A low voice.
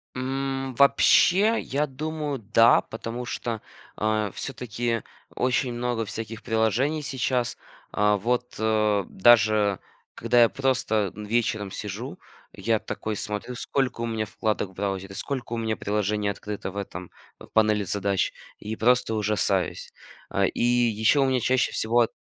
Yes: low, 115 Hz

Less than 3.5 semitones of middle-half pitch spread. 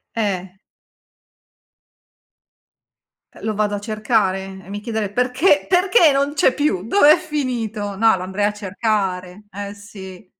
No: average, 4.3 semitones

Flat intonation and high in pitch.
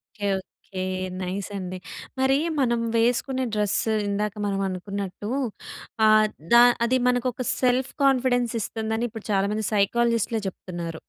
No: average, 3.7 semitones; high, 215 Hz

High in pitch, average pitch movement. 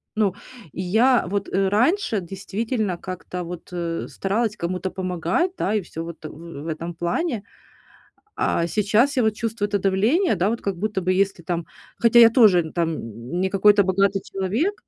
Yes: high, 195 Hz; average, 3.9 semitones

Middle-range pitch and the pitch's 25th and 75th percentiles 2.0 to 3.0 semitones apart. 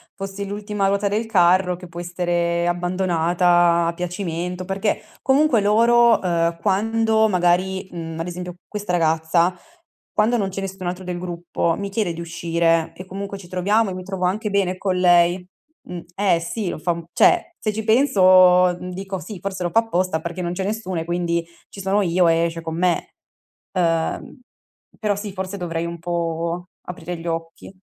Yes: medium, 180 Hz; narrow, 2.6 semitones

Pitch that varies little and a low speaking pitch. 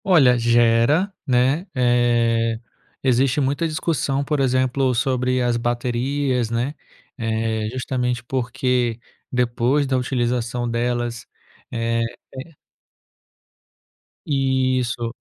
Yes: narrow, 2.1 semitones; low, 125 Hz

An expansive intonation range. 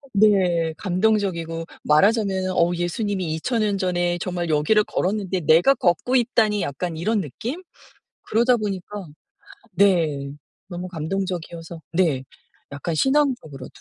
No: average, 4.1 semitones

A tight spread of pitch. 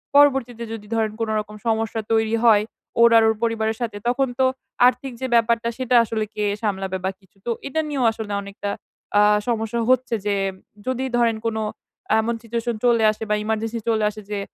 Yes: narrow, 1.7 semitones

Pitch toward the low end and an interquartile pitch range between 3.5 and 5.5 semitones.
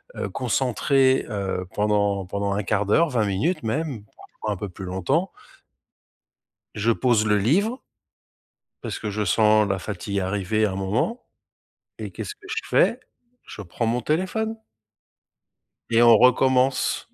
Yes: low, 110 Hz; average, 4.6 semitones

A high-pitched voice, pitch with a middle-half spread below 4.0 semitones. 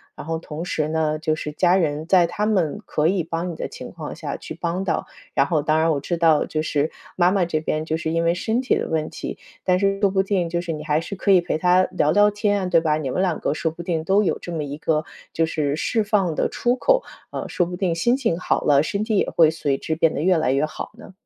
No: medium, 165 Hz; average, 3.3 semitones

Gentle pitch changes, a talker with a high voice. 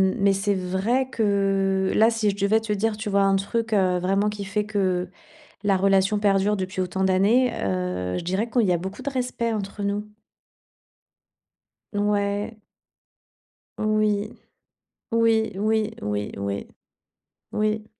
Yes: narrow, 2.1 semitones; high, 200 Hz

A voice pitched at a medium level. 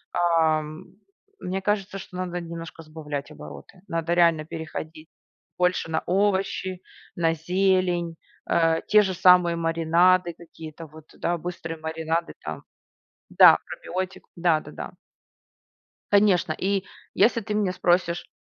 Yes: medium, 170 Hz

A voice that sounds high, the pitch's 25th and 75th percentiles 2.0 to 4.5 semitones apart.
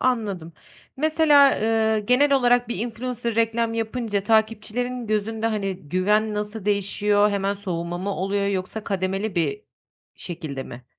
Yes: high, 215 Hz; average, 3.0 semitones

